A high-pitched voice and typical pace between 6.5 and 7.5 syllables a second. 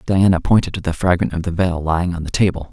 No: very low, 90 Hz; 6.6 syllables/s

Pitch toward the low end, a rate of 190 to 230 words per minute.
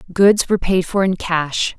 No: medium, 185 Hz; average, 200 wpm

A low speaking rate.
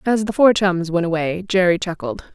No: fast, 205 wpm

